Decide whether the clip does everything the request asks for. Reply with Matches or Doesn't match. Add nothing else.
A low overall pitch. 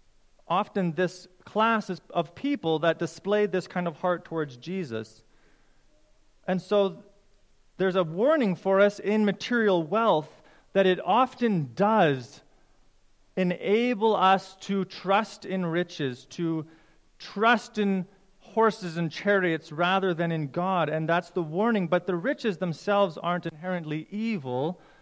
Doesn't match